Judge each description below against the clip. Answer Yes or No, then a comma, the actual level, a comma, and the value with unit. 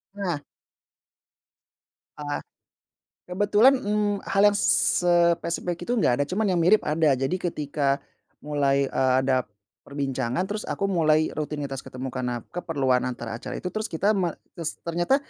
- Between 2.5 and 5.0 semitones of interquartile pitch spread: No, wide, 5.4 semitones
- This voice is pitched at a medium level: Yes, medium, 155 Hz